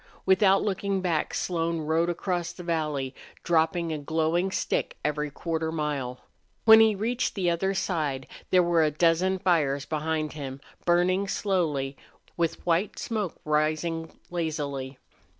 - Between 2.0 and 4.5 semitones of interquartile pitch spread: Yes, average, 3.2 semitones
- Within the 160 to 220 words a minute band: No, average, 145 wpm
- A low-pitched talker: No, medium, 165 Hz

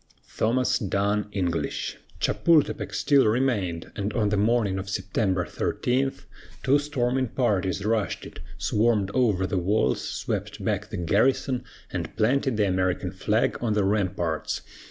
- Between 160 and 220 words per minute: No, slow, 135 wpm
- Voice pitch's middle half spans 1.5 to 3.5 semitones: No, average, 4.5 semitones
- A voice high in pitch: No, low, 105 Hz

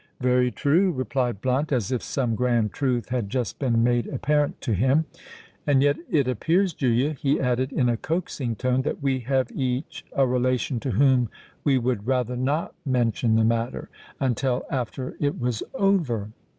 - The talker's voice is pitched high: No, low, 130 Hz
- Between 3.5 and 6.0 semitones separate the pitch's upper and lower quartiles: No, narrow, 2.5 semitones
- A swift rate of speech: No, average, 165 wpm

